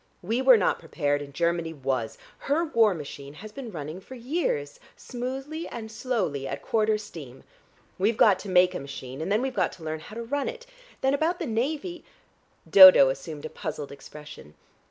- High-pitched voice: Yes, high, 195 Hz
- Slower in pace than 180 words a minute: No, average, 190 wpm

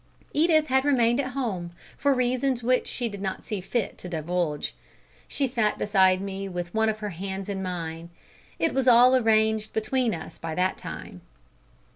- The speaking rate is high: No, average, 175 wpm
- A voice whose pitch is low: No, high, 215 Hz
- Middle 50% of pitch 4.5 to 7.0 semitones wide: Yes, average, 5.3 semitones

